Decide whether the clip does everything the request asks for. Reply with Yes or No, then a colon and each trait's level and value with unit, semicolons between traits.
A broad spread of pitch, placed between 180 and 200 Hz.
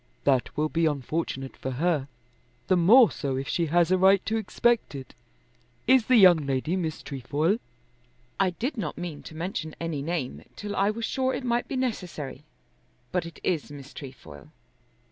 No: wide, 5.8 semitones; medium, 170 Hz